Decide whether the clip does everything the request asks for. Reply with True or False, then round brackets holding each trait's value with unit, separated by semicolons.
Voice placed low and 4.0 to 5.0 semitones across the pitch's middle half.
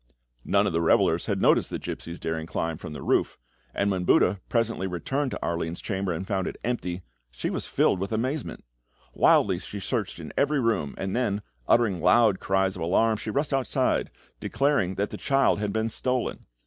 True (100 Hz; 4.7 semitones)